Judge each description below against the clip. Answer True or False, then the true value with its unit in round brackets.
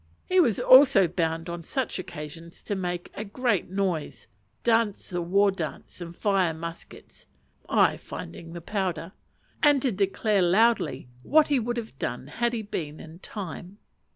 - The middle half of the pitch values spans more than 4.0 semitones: True (5.0 semitones)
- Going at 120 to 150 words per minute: False (160 wpm)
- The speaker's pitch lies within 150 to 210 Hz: True (190 Hz)